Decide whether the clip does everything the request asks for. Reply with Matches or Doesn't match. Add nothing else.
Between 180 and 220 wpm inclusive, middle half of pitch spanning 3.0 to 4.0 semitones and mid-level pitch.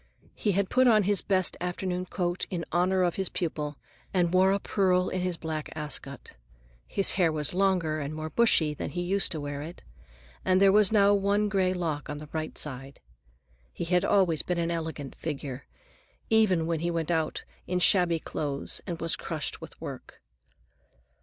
Matches